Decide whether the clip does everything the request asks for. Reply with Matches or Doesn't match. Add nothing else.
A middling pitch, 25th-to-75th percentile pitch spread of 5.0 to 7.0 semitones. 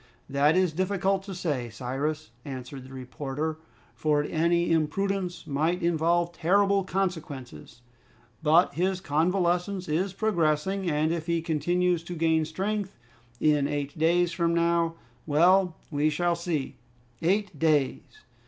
Doesn't match